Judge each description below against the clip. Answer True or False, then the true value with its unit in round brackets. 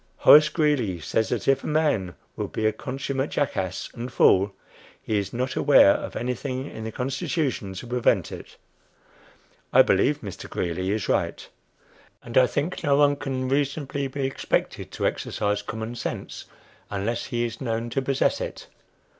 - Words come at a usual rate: True (165 wpm)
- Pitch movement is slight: False (4.0 semitones)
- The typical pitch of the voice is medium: False (125 Hz)